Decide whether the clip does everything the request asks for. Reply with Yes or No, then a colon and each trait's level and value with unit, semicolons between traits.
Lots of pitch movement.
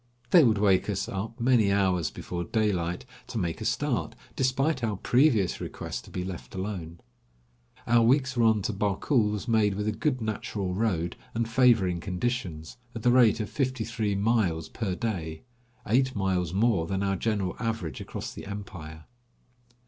No: average, 4.1 semitones